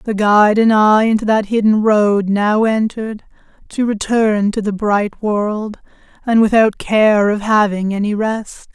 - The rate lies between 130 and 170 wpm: Yes, average, 160 wpm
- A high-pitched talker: Yes, high, 210 Hz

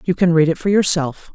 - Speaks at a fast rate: Yes, fast, 270 wpm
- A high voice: No, medium, 170 Hz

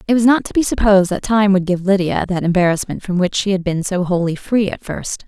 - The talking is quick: Yes, fast, 260 wpm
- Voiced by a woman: Yes, female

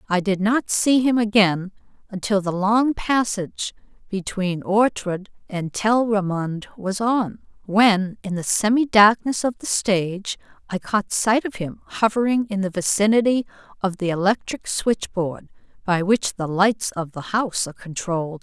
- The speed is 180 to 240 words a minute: No, average, 155 wpm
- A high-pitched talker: Yes, high, 205 Hz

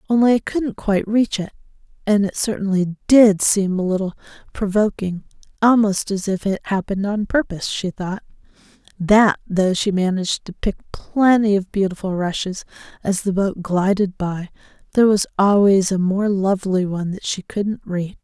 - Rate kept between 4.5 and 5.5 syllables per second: Yes, 4.7 syllables/s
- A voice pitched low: No, high, 195 Hz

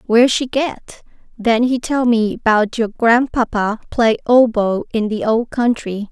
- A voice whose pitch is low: No, high, 230 Hz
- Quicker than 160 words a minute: No, average, 155 wpm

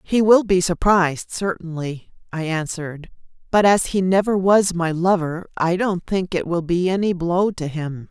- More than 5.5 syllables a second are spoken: No, 4.5 syllables/s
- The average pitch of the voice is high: No, medium, 175 Hz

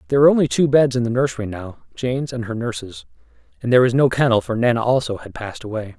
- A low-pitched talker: Yes, low, 120 Hz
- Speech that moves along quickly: Yes, fast, 240 wpm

